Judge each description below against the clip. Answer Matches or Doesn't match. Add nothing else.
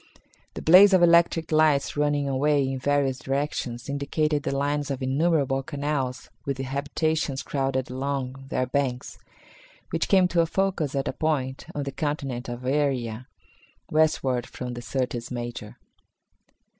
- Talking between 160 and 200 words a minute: Doesn't match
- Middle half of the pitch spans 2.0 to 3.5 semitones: Matches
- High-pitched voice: Doesn't match